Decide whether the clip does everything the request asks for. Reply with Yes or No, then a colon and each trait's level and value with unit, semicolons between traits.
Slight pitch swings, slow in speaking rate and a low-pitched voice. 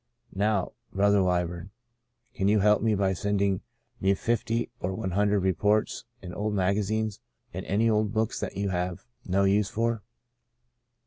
No: narrow, 1.9 semitones; average, 150 wpm; low, 100 Hz